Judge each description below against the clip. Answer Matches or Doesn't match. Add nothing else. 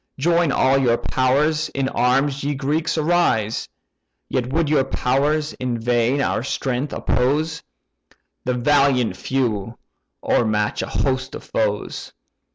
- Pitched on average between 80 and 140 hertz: Matches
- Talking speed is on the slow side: Matches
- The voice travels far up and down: Doesn't match